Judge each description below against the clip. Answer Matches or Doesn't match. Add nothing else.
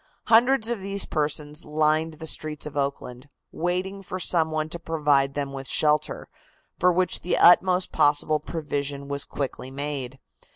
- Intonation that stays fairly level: Doesn't match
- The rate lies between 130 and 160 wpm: Matches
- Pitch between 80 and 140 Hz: Doesn't match